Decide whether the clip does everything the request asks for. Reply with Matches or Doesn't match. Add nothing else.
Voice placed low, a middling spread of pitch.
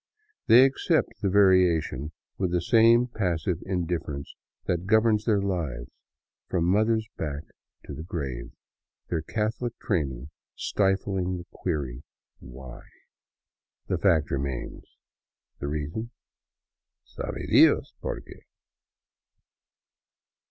Doesn't match